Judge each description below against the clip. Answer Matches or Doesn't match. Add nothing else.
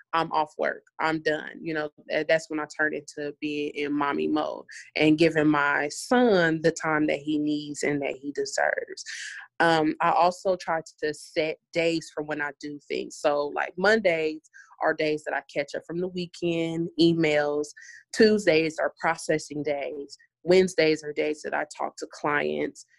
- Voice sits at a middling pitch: Matches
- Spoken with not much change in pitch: Matches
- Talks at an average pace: Matches